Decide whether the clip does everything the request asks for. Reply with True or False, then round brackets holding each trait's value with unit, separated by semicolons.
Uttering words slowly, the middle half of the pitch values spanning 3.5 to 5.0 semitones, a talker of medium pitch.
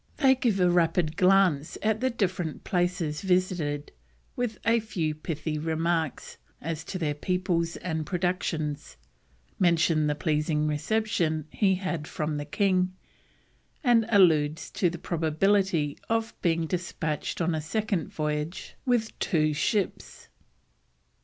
True (130 wpm; 3.9 semitones; 170 Hz)